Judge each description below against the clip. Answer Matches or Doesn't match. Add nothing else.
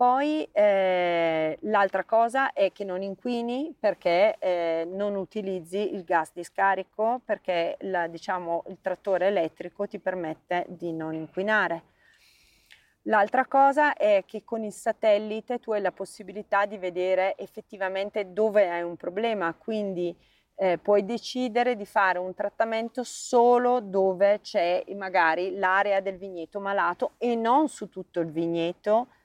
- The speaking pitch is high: Matches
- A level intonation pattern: Doesn't match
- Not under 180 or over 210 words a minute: Doesn't match